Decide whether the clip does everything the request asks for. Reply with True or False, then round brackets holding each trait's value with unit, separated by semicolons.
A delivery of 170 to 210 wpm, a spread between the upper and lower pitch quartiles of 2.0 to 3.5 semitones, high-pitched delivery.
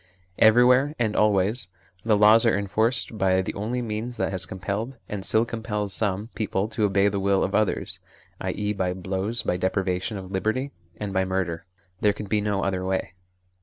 False (180 wpm; 2.6 semitones; 105 Hz)